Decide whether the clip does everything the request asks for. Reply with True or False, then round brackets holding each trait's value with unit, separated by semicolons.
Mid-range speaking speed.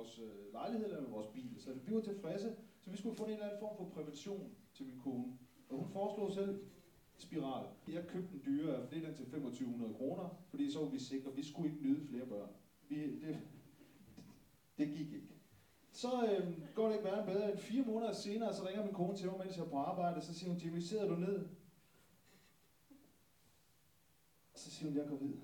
True (210 wpm)